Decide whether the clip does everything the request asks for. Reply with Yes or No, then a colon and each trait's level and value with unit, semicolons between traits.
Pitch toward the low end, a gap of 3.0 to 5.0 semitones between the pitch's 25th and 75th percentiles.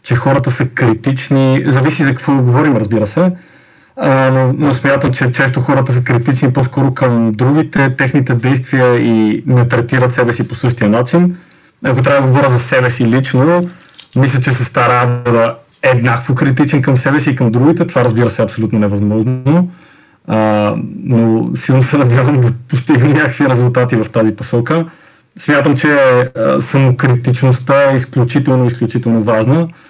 No: low, 130 Hz; narrow, 2.4 semitones